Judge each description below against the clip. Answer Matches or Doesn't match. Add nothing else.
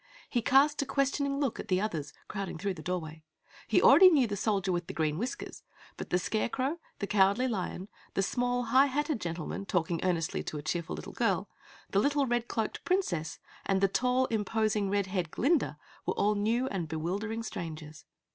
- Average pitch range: Doesn't match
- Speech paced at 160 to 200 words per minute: Matches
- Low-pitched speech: Doesn't match